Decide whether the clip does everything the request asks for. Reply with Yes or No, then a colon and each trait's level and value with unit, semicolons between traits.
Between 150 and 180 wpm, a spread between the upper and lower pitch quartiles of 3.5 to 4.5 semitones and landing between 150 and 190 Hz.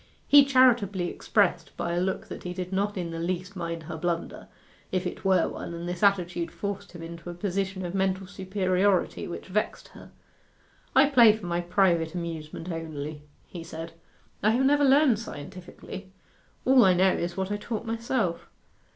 No: average, 175 wpm; average, 3.0 semitones; medium, 185 Hz